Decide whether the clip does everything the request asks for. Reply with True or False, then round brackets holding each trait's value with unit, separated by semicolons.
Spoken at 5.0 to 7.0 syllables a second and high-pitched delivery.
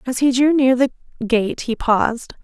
False (4.7 syllables/s; 250 Hz)